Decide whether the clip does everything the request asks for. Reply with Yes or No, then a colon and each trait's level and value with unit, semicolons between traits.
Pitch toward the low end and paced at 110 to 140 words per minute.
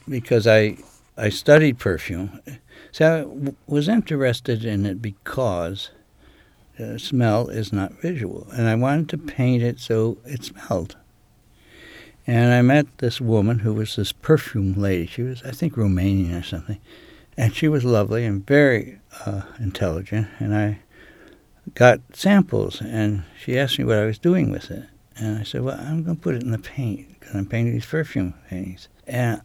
No: low, 115 Hz; average, 175 wpm